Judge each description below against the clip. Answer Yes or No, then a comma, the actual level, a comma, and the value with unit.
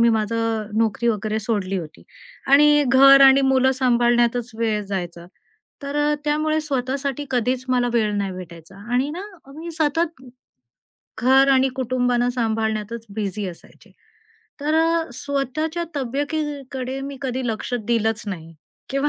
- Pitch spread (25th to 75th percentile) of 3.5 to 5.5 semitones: Yes, average, 4.1 semitones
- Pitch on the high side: Yes, very high, 250 Hz